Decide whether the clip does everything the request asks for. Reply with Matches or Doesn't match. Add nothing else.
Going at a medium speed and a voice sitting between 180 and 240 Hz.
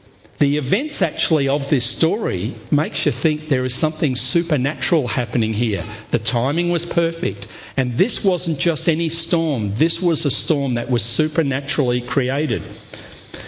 Doesn't match